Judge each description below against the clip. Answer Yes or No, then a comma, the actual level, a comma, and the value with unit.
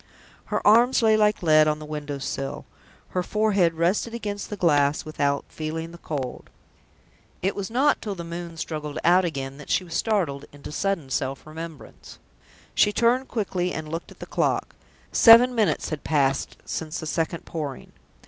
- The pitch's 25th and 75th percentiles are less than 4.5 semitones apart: No, average, 5.1 semitones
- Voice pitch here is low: No, medium, 165 Hz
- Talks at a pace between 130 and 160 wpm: No, average, 170 wpm